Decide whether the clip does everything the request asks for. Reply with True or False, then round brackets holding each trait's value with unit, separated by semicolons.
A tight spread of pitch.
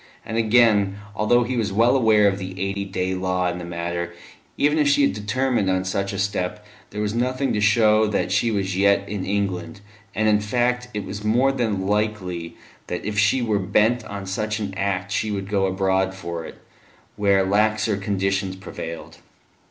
True (2.3 semitones)